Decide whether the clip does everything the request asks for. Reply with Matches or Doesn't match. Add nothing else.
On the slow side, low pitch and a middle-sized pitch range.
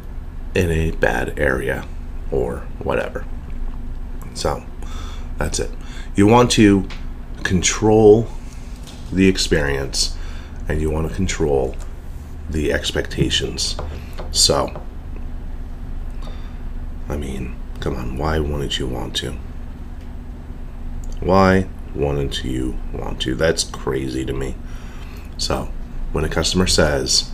Matches